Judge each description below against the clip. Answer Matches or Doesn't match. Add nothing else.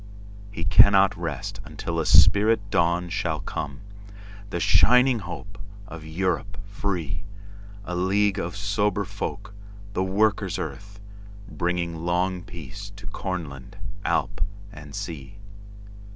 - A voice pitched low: Matches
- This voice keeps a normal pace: Doesn't match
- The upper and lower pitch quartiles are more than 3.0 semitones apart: Doesn't match